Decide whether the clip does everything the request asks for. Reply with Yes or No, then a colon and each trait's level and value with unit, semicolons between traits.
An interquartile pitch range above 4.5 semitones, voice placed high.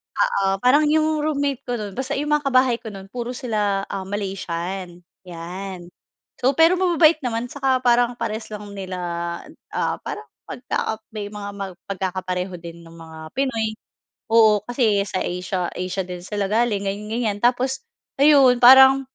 Yes: average, 5.1 semitones; high, 215 Hz